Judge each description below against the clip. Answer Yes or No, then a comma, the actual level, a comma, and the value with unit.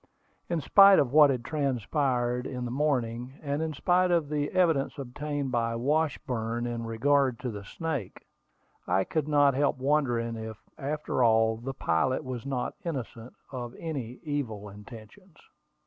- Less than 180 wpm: Yes, average, 150 wpm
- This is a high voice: No, low, 130 Hz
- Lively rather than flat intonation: No, average, 4.1 semitones